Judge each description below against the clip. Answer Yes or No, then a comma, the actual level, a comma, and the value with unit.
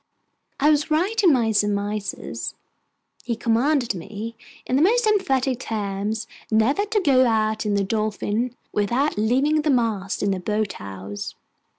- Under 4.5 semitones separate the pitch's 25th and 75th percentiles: No, wide, 5.4 semitones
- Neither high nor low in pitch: No, high, 225 Hz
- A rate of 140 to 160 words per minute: Yes, average, 150 wpm